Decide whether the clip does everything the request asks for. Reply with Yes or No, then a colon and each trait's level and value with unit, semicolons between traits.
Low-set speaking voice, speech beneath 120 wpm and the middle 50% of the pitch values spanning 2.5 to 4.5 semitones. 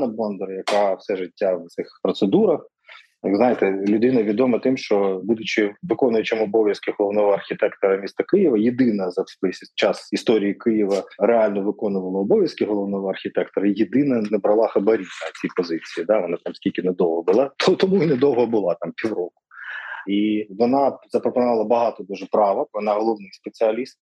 No: low, 105 Hz; average, 145 wpm; average, 3.3 semitones